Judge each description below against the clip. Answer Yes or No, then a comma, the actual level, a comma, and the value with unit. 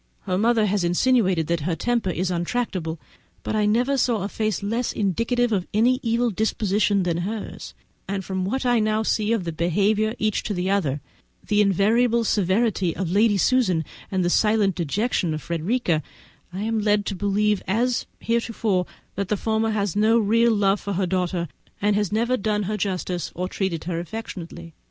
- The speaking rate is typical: Yes, average, 185 wpm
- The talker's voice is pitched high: Yes, high, 205 Hz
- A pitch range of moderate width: Yes, average, 3.5 semitones